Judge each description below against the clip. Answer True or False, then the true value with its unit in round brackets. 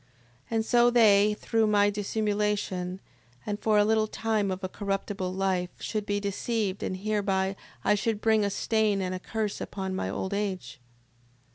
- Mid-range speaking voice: False (205 Hz)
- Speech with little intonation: True (2.0 semitones)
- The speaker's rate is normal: True (165 wpm)